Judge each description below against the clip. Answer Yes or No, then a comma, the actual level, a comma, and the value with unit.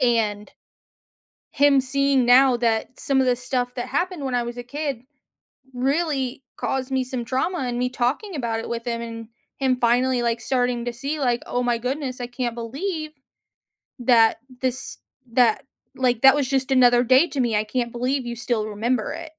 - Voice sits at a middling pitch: No, very high, 250 Hz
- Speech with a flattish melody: Yes, narrow, 2.0 semitones